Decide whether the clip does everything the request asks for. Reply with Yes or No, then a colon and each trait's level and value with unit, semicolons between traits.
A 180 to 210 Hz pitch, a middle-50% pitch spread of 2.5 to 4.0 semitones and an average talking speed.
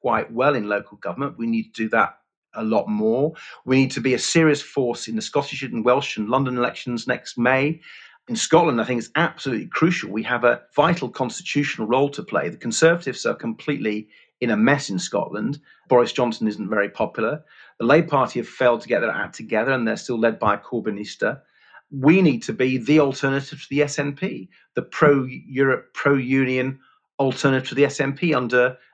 No: low, 135 Hz; average, 3.4 semitones; average, 195 wpm